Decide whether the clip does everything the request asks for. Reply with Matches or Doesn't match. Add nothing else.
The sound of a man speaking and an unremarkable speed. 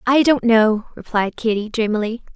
Doesn't match